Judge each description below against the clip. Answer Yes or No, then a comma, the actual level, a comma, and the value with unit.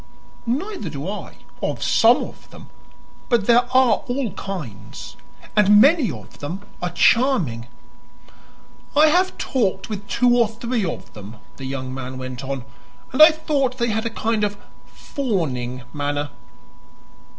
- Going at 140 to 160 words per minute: Yes, average, 145 wpm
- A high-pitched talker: Yes, high, 210 Hz